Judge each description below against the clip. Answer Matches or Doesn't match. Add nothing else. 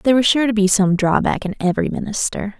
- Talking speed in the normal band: Doesn't match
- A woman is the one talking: Matches